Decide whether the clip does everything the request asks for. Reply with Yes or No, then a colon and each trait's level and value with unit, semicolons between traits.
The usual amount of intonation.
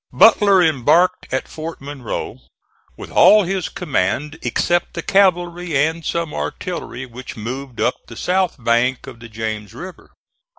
No: wide, 6.2 semitones